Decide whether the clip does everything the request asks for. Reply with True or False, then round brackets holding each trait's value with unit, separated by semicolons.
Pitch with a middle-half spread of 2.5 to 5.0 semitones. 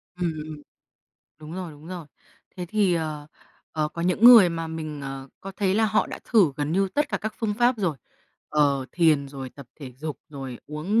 True (4.7 semitones)